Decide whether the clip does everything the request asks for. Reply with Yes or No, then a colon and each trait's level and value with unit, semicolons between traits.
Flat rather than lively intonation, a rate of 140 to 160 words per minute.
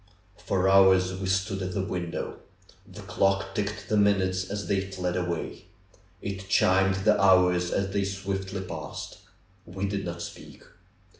Yes: narrow, 1.1 semitones; average, 150 wpm